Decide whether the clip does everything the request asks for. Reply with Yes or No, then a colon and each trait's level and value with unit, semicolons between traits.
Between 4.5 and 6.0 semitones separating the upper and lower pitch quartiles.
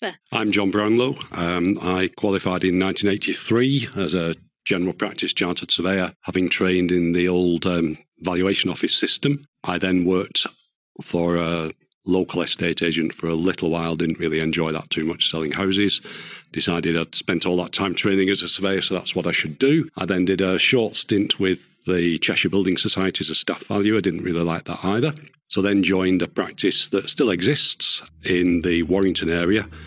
No: narrow, 2.4 semitones